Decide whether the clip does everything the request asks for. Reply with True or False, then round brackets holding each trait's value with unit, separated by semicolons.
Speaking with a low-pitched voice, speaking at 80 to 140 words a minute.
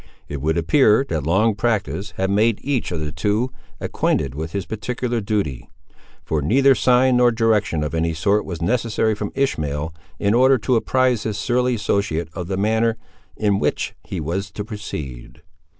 False (105 Hz; 170 wpm)